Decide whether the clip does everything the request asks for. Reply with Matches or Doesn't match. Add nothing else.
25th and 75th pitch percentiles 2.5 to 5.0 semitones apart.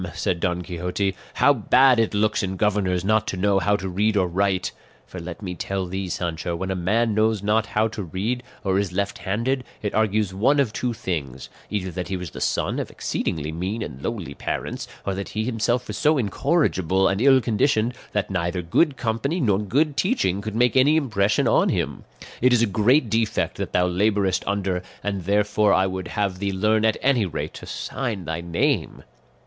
Matches